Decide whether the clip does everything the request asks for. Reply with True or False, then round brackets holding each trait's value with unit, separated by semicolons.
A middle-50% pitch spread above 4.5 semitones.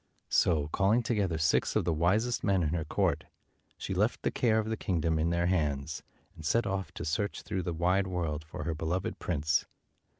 False (3.6 semitones)